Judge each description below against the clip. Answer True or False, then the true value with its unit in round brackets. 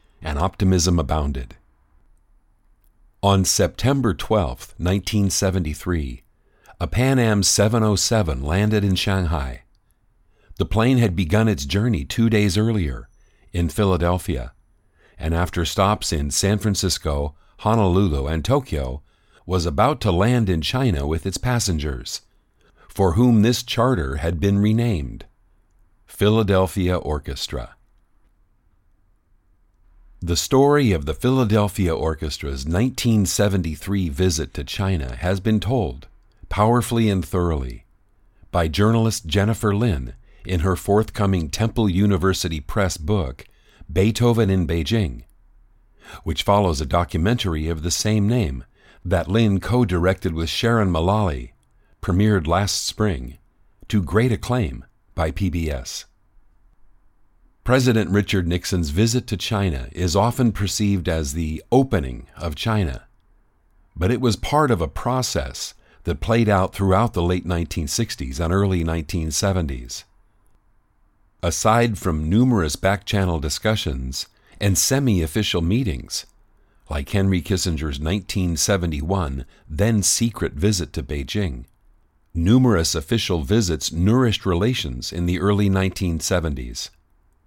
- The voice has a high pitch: False (95 Hz)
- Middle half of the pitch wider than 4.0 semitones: True (4.5 semitones)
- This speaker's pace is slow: True (110 wpm)